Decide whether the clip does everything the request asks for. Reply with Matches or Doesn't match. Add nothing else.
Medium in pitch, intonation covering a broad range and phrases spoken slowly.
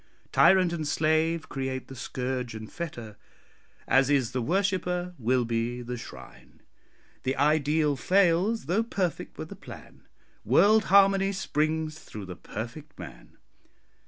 Matches